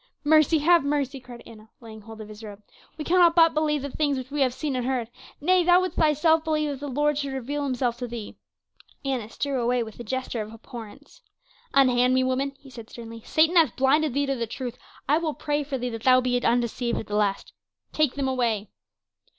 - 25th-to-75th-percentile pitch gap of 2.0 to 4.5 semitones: Yes, average, 3.9 semitones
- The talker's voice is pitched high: Yes, very high, 260 Hz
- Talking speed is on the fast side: Yes, fast, 220 wpm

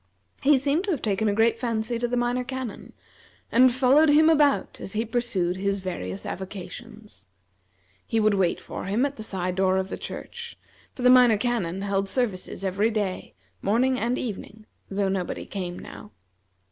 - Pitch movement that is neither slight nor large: Yes, average, 4.5 semitones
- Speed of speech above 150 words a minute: Yes, average, 175 wpm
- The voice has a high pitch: Yes, high, 220 Hz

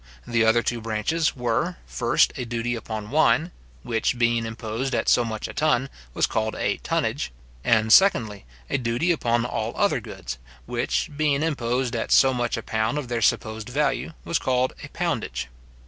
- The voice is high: No, low, 120 Hz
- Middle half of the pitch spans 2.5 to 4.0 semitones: Yes, average, 3.2 semitones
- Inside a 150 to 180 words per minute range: Yes, average, 175 wpm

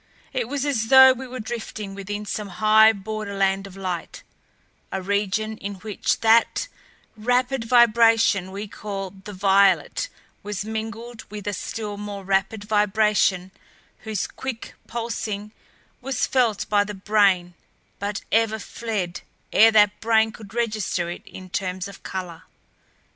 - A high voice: Yes, high, 210 Hz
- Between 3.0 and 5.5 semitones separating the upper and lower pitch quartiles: No, narrow, 2.4 semitones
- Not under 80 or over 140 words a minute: Yes, slow, 135 wpm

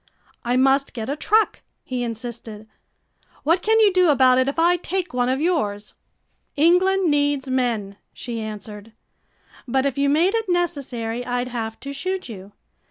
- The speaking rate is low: No, average, 165 wpm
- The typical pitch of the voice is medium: No, very high, 265 Hz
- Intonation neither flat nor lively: No, wide, 6.5 semitones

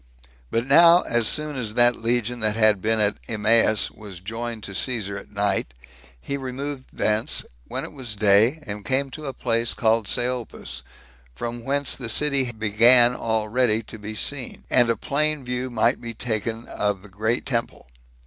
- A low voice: Yes, low, 115 Hz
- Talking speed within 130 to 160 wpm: No, average, 170 wpm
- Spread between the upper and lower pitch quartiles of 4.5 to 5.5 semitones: No, average, 2.9 semitones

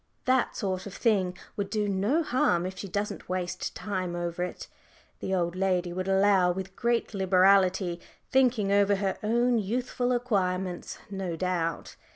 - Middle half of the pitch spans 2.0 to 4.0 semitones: Yes, narrow, 2.5 semitones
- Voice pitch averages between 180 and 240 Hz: Yes, high, 190 Hz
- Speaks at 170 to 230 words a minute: No, average, 155 wpm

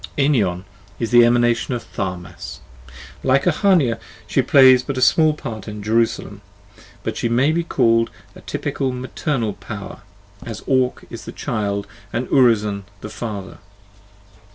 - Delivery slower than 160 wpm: Yes, average, 140 wpm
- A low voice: Yes, low, 120 Hz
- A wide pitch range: No, average, 3.7 semitones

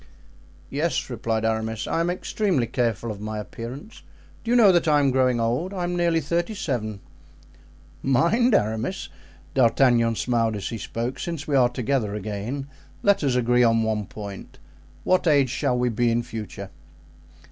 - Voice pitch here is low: Yes, low, 125 Hz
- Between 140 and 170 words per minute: Yes, average, 160 wpm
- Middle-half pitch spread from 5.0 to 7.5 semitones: Yes, wide, 5.6 semitones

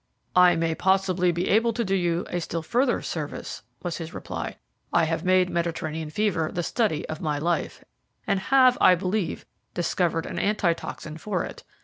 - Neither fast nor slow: Yes, average, 170 wpm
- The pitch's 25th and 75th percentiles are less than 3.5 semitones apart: Yes, average, 2.9 semitones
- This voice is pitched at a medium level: Yes, medium, 175 Hz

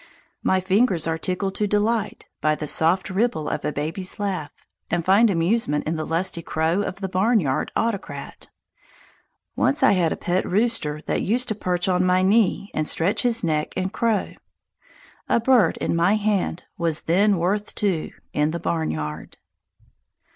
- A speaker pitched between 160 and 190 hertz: Yes, medium, 185 Hz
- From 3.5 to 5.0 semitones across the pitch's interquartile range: Yes, average, 4.2 semitones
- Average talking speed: Yes, average, 165 wpm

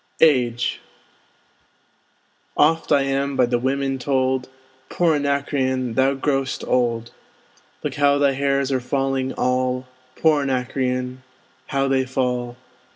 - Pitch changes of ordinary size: No, narrow, 1.6 semitones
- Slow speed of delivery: Yes, slow, 115 wpm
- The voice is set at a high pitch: No, low, 135 Hz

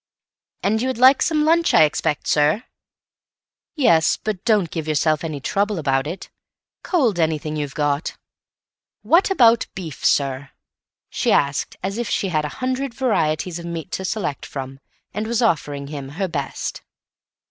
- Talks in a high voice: No, medium, 170 Hz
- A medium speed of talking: Yes, average, 160 wpm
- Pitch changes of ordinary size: No, wide, 7.3 semitones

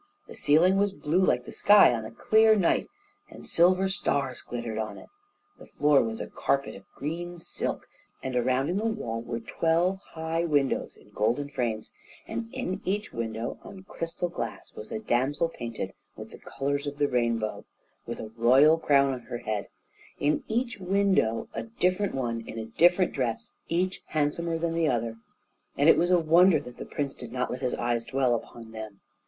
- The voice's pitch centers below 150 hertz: Yes, medium, 140 Hz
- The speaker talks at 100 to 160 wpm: No, average, 190 wpm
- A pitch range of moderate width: No, wide, 6.8 semitones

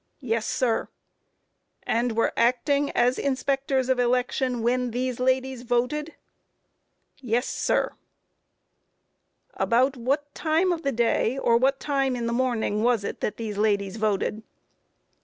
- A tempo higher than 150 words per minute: No, average, 145 wpm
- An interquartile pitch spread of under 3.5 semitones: Yes, narrow, 2.5 semitones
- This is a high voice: Yes, very high, 250 Hz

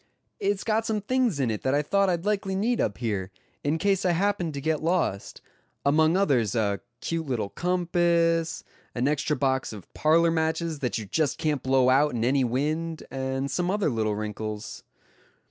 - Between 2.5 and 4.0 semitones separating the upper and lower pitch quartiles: No, wide, 5.4 semitones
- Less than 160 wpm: No, average, 180 wpm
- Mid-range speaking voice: Yes, medium, 155 Hz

